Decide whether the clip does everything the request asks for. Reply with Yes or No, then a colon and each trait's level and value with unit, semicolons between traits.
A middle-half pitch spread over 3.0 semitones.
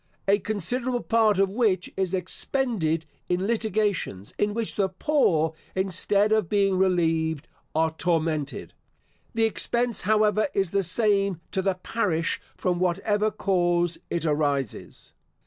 Yes: average, 4.1 semitones